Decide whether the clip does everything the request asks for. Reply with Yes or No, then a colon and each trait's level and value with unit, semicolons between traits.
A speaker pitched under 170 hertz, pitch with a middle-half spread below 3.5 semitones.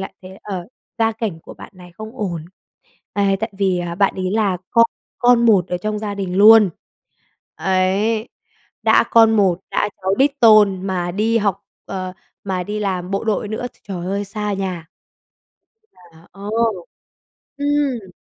No: high, 200 Hz; average, 2.8 semitones